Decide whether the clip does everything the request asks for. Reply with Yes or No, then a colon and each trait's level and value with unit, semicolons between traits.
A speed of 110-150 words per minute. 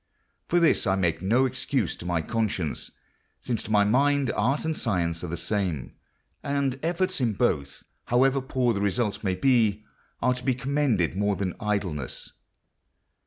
No: average, 165 wpm